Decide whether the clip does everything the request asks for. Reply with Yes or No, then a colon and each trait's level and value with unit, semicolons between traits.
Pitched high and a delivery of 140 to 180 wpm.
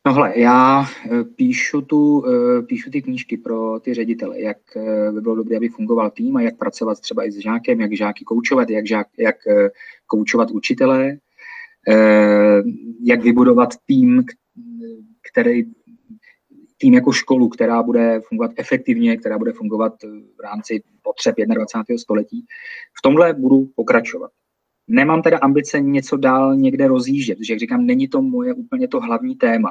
Yes: high, 225 Hz; average, 145 wpm